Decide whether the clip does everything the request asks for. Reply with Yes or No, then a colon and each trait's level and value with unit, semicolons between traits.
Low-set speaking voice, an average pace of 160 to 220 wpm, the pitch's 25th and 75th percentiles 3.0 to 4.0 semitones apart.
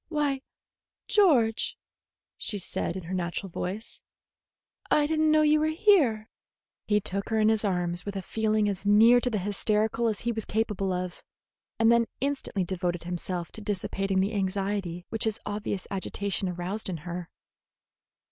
No: high, 205 Hz; average, 165 wpm; average, 3.4 semitones